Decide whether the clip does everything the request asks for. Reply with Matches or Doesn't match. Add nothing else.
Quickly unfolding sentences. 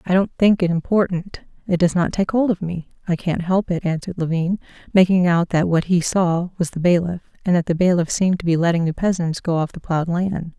Matches